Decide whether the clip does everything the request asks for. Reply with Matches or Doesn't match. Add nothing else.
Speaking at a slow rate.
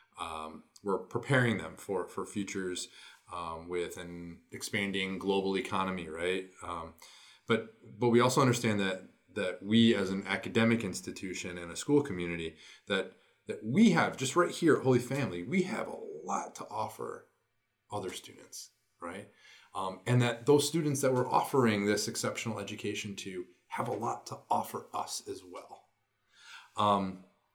Doesn't match